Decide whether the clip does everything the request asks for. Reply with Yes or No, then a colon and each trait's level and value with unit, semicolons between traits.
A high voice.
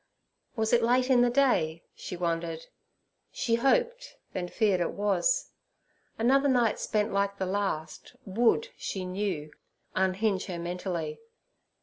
Yes: high, 200 Hz